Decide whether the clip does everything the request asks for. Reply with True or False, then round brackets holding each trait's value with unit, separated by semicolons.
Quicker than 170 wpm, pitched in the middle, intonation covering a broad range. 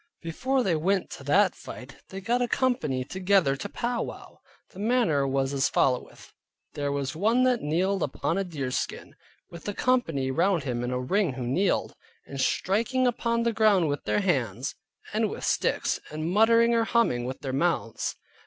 True (180 wpm; 175 Hz; 8.5 semitones)